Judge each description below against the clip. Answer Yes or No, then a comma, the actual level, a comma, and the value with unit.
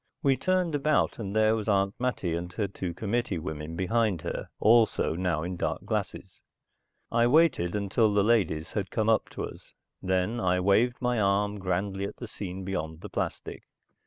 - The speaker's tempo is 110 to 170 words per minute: No, average, 180 wpm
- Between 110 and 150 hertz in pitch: No, low, 100 Hz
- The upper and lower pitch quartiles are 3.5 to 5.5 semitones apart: Yes, average, 4.1 semitones